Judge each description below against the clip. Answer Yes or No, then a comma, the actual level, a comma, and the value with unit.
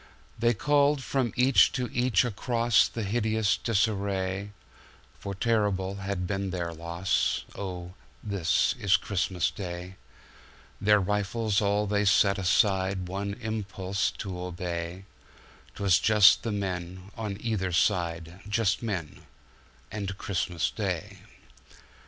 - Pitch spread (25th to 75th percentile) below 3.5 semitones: Yes, narrow, 2.6 semitones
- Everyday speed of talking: No, slow, 100 wpm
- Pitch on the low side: Yes, low, 100 Hz